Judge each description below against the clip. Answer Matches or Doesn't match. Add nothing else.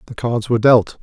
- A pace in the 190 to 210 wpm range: Doesn't match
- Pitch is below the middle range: Matches